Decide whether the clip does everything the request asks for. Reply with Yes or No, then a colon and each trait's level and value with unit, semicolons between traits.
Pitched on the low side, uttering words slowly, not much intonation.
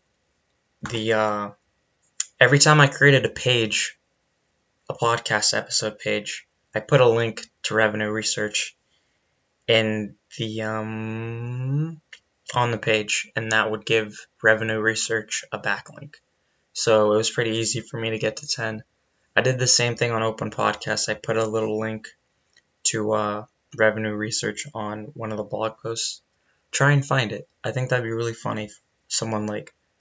No: low, 110 Hz; average, 160 wpm; narrow, 1.4 semitones